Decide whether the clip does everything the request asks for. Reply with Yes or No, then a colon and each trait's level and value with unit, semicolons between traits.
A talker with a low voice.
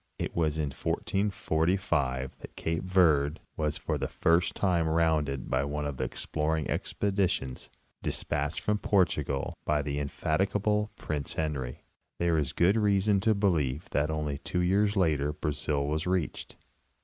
Yes: very low, 80 Hz